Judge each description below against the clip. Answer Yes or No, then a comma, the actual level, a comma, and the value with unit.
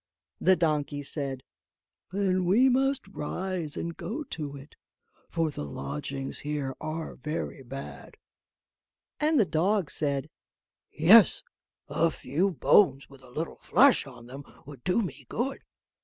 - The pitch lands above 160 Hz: No, medium, 155 Hz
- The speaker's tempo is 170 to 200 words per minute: No, slow, 135 wpm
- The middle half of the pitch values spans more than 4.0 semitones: Yes, wide, 5.6 semitones